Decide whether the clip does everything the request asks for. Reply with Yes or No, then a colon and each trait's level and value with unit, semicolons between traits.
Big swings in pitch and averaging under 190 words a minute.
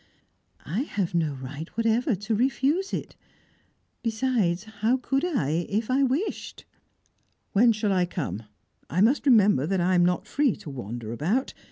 Yes: wide, 6.7 semitones; average, 155 wpm